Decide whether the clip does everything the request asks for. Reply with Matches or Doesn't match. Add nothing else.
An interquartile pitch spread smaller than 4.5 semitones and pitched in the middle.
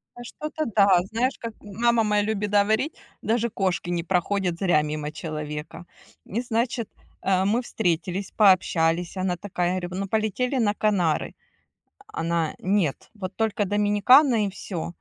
Doesn't match